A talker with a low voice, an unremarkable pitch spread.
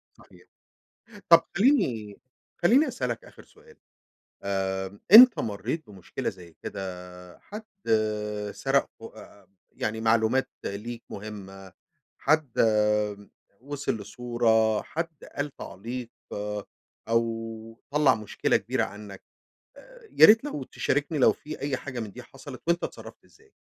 No: low, 120 Hz; wide, 6.8 semitones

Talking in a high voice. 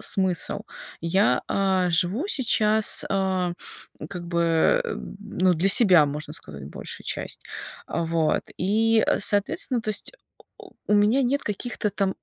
Yes: high, 195 Hz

